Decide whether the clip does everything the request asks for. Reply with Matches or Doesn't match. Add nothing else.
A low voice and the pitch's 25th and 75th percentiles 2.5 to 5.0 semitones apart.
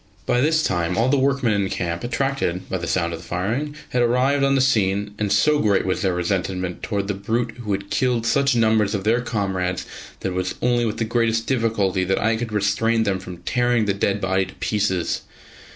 Matches